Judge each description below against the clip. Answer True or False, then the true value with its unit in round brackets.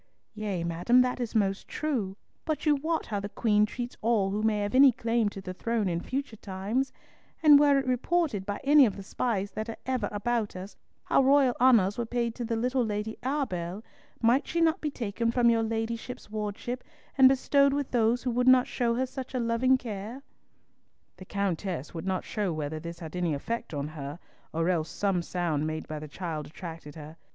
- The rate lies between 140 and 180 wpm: False (200 wpm)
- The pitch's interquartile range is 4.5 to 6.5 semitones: True (5.1 semitones)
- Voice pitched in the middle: False (220 Hz)